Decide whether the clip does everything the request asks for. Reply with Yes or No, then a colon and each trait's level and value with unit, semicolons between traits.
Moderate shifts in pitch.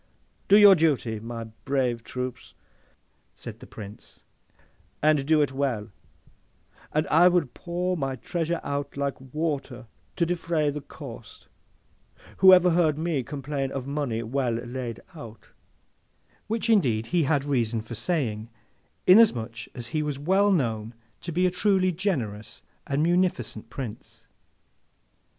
No: wide, 6.0 semitones